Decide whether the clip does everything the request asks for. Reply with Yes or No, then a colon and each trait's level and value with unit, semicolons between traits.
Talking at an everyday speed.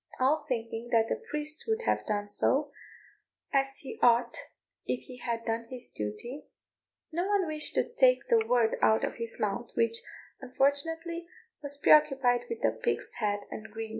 Yes: average, 165 wpm